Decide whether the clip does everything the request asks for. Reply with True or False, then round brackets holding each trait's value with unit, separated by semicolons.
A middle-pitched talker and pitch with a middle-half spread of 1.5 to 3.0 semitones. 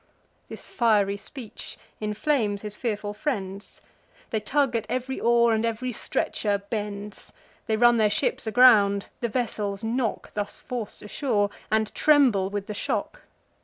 False (220 Hz; 2.7 semitones)